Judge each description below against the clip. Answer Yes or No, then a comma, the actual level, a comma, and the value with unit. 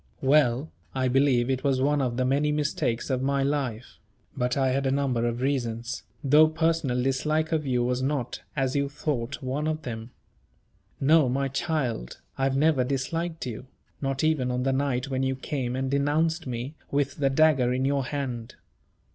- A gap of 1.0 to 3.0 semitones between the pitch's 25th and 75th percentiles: Yes, narrow, 2.5 semitones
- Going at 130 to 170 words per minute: No, average, 180 wpm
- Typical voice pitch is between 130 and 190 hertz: Yes, low, 135 Hz